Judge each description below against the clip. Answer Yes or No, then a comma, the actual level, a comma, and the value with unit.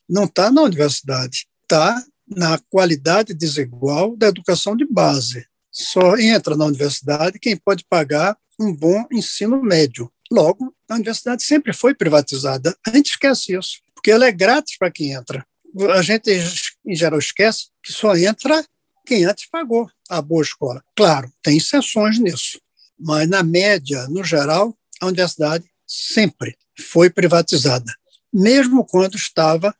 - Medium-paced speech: Yes, average, 145 wpm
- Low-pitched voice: No, medium, 185 Hz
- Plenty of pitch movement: Yes, wide, 6.2 semitones